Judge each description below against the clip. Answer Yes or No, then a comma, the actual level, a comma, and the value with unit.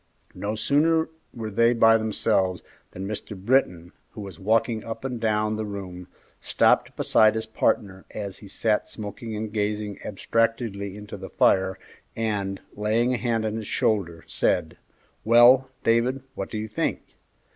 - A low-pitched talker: Yes, low, 110 Hz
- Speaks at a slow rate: No, average, 155 wpm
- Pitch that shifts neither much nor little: No, narrow, 2.3 semitones